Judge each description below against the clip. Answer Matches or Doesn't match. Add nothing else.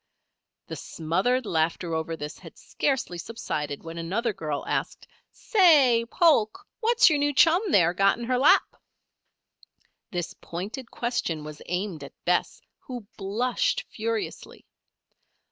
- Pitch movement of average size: Doesn't match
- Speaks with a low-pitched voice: Doesn't match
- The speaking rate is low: Matches